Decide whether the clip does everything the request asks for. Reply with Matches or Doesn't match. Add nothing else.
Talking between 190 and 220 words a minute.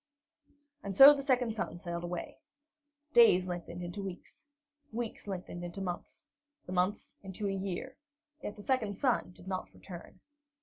Doesn't match